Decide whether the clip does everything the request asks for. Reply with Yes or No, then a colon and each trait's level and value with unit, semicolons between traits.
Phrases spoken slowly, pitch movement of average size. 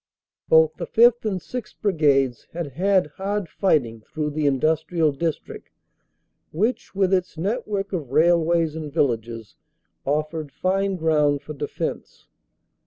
Yes: slow, 130 wpm; average, 4.5 semitones